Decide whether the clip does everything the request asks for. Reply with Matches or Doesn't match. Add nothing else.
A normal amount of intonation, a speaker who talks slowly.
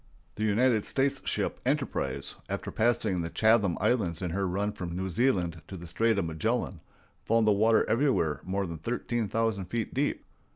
Doesn't match